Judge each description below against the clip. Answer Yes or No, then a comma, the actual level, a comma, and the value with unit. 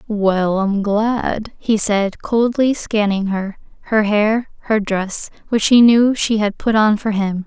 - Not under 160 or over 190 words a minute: Yes, average, 170 wpm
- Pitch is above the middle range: Yes, high, 210 Hz